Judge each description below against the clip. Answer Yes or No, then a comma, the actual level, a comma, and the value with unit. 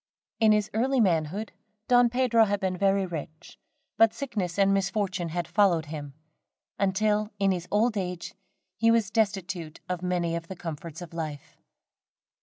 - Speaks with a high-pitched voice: Yes, high, 195 Hz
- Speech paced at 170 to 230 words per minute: No, average, 155 wpm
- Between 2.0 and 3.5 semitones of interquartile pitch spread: No, average, 3.9 semitones